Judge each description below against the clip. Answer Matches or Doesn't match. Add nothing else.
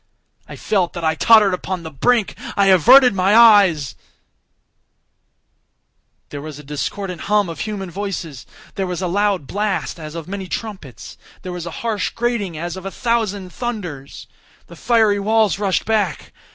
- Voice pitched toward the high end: Matches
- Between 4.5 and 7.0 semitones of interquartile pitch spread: Doesn't match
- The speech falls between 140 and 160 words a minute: Matches